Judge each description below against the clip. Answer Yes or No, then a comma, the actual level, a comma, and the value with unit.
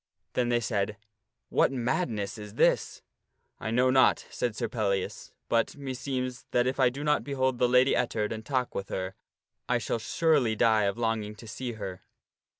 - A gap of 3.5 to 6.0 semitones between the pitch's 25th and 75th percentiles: No, average, 3.1 semitones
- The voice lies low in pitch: Yes, low, 120 Hz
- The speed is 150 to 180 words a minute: No, average, 190 wpm